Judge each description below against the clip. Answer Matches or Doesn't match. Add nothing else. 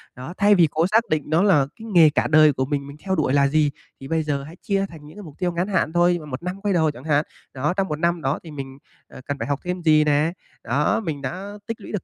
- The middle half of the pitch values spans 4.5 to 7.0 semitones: Doesn't match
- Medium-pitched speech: Matches